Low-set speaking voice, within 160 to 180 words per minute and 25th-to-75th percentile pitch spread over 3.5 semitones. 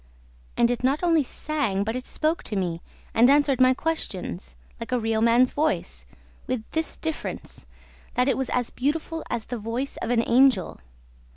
No: very high, 250 Hz; average, 175 wpm; average, 4.1 semitones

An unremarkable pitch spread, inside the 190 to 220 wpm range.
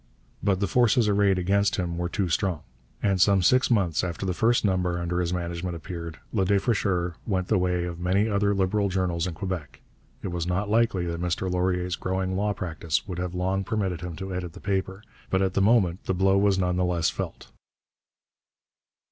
No: narrow, 2.1 semitones; average, 200 wpm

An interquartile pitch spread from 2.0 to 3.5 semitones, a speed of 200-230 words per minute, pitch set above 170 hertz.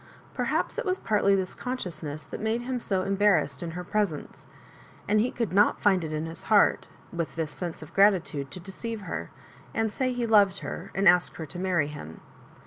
No: average, 4.4 semitones; fast, 205 wpm; high, 190 Hz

